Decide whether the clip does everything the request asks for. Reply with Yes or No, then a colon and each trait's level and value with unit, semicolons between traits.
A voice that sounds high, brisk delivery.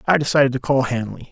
No: low, 135 Hz; fast, 230 wpm